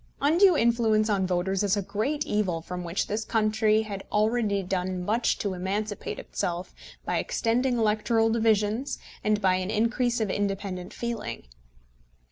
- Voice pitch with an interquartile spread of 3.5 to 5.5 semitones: No, average, 3.0 semitones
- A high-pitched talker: Yes, high, 215 Hz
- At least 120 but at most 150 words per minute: Yes, average, 145 wpm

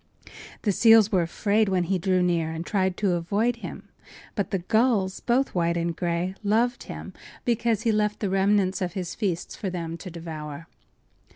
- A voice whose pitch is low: No, high, 190 Hz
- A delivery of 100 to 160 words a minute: No, average, 180 wpm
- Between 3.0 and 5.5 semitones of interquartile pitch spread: Yes, average, 3.8 semitones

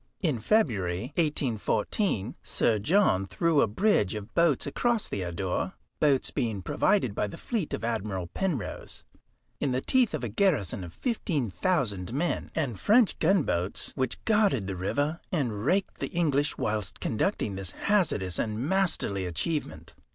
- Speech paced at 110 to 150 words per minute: Yes, average, 145 wpm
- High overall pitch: No, low, 130 Hz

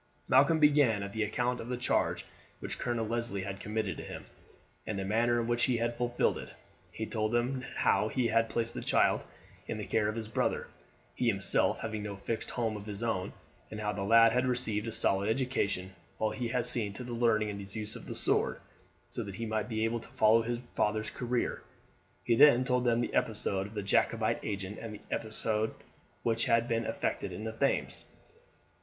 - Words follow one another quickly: Yes, fast, 210 wpm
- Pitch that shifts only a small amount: Yes, narrow, 2.1 semitones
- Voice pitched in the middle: No, low, 115 Hz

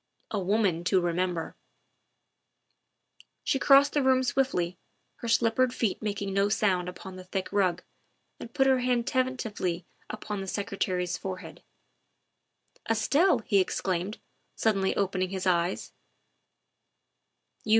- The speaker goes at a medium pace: No, slow, 120 wpm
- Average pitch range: Yes, average, 4.4 semitones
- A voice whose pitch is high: Yes, high, 200 Hz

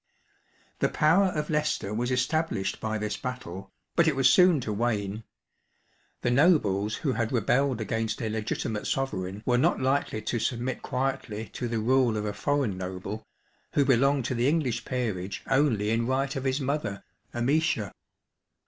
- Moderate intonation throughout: Yes, average, 4.1 semitones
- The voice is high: No, low, 120 Hz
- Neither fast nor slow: Yes, average, 160 wpm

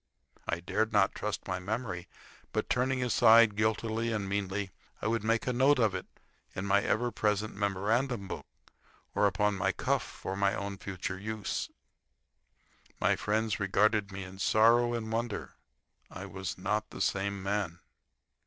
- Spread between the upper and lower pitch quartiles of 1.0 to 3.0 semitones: Yes, narrow, 2.4 semitones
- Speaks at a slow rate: No, average, 155 wpm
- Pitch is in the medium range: No, low, 105 Hz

